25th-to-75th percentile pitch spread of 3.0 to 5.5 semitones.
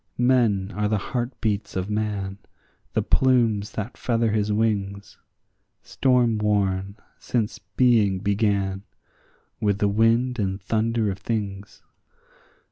No: narrow, 2.5 semitones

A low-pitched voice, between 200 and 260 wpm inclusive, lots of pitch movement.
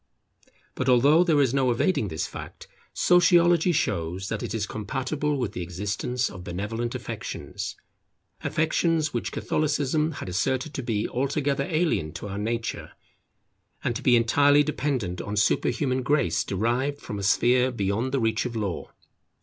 No: low, 125 Hz; average, 150 wpm; wide, 5.9 semitones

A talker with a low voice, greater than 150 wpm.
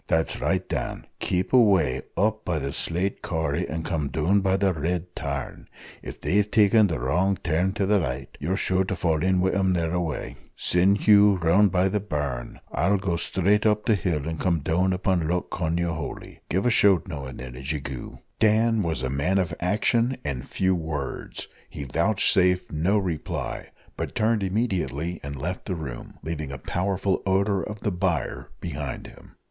Yes: very low, 90 Hz; average, 185 wpm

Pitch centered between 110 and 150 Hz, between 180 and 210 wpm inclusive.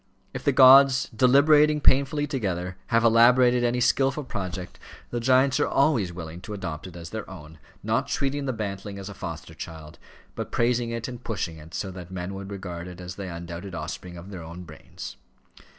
No: low, 100 Hz; average, 190 wpm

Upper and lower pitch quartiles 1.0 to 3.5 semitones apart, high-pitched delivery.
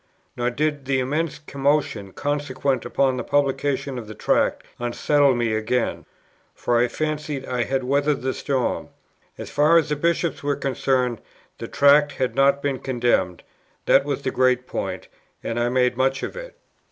No: narrow, 2.5 semitones; low, 135 Hz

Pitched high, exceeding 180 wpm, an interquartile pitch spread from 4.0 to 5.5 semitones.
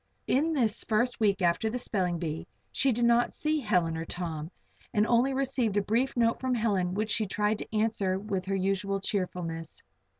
Yes: high, 210 Hz; average, 190 wpm; average, 4.3 semitones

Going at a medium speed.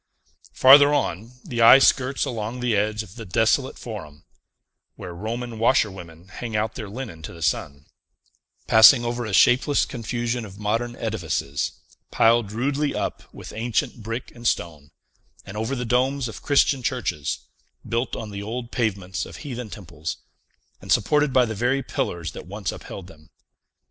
Yes: average, 160 wpm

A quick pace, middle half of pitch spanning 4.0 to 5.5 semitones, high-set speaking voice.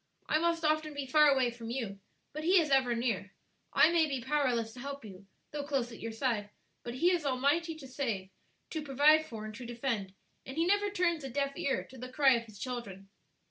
Yes: fast, 220 wpm; average, 4.6 semitones; very high, 265 Hz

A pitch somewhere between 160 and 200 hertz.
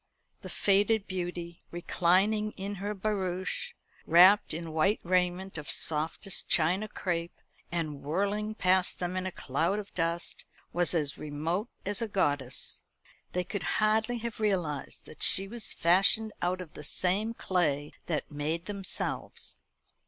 Yes: medium, 185 Hz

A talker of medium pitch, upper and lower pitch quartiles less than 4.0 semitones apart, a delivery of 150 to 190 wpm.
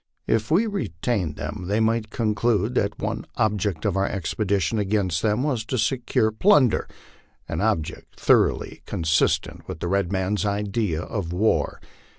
No: low, 105 Hz; average, 3.2 semitones; average, 155 wpm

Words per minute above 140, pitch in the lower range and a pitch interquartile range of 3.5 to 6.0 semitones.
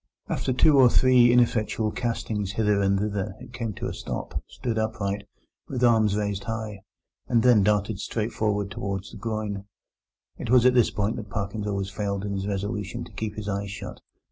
No: average, 190 wpm; low, 105 Hz; narrow, 2.4 semitones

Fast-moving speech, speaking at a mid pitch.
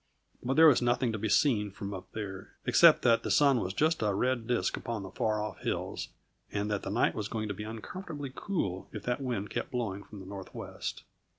No: fast, 220 wpm; low, 110 Hz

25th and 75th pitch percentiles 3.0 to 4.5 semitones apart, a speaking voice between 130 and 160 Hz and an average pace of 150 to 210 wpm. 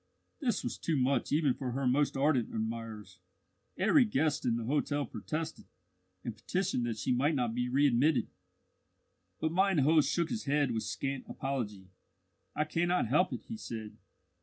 No: average, 5.0 semitones; medium, 140 Hz; average, 160 wpm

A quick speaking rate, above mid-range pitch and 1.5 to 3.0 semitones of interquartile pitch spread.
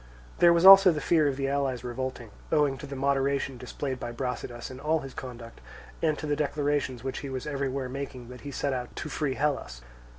No: fast, 210 wpm; low, 135 Hz; narrow, 2.5 semitones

